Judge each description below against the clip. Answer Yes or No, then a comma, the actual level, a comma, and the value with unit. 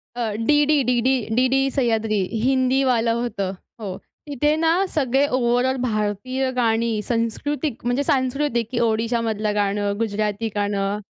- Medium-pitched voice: No, high, 240 Hz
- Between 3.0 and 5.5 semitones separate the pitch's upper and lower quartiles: Yes, average, 3.6 semitones